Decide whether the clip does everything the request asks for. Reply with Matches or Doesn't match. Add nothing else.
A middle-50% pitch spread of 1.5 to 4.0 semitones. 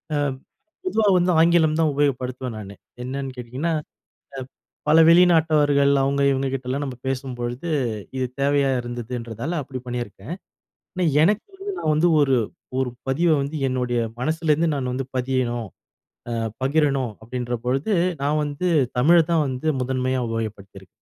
Matches